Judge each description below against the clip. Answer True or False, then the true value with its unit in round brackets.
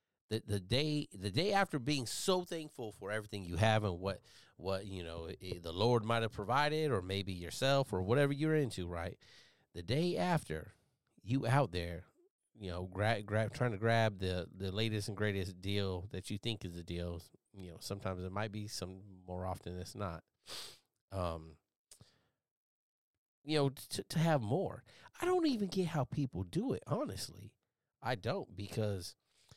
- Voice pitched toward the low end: True (105 Hz)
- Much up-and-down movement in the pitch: True (6.3 semitones)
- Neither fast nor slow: True (175 wpm)